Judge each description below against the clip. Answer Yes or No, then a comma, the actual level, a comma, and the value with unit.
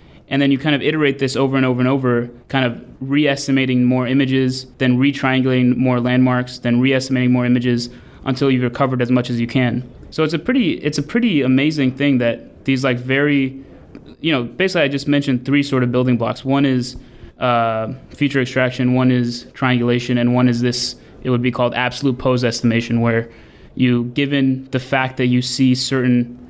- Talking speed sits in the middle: Yes, average, 190 wpm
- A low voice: Yes, low, 130 Hz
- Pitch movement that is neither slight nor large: No, narrow, 1.6 semitones